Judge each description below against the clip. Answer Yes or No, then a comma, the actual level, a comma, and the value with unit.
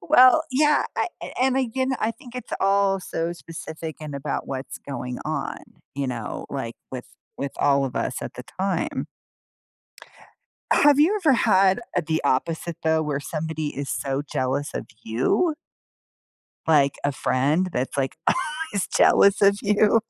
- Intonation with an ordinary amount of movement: No, wide, 7.6 semitones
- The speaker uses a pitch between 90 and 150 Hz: No, medium, 160 Hz